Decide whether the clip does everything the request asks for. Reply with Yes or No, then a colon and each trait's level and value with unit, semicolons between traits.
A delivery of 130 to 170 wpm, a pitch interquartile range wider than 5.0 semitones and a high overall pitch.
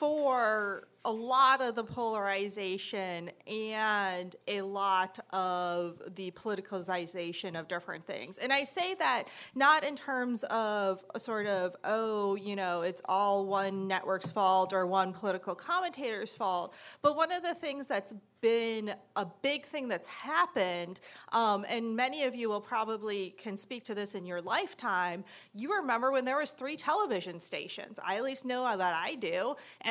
Yes: average, 165 wpm; wide, 5.5 semitones; high, 210 Hz